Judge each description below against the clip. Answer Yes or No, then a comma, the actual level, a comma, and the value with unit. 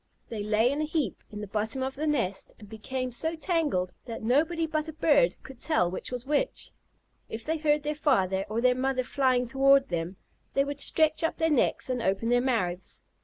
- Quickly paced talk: Yes, fast, 210 wpm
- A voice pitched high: Yes, very high, 260 Hz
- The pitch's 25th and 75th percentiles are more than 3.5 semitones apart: Yes, average, 5.3 semitones